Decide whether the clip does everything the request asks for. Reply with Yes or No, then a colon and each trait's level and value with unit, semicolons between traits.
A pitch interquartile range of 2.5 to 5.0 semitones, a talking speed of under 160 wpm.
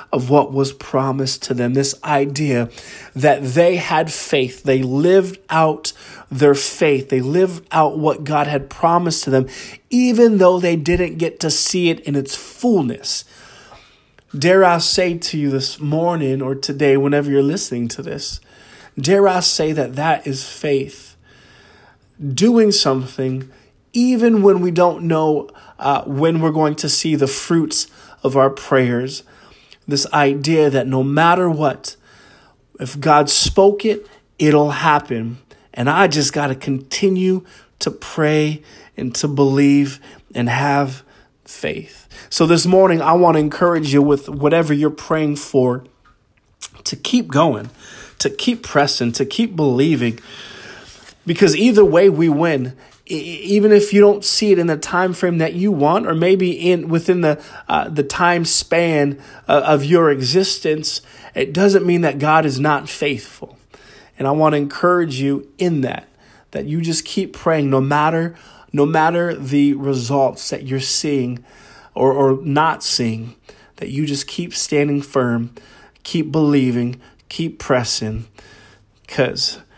Yes: average, 3.9 semitones; average, 150 wpm